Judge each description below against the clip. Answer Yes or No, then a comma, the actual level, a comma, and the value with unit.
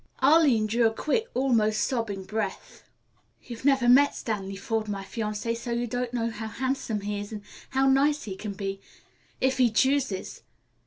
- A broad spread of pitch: No, average, 3.9 semitones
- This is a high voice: Yes, high, 230 Hz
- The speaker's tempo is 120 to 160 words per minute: No, average, 170 wpm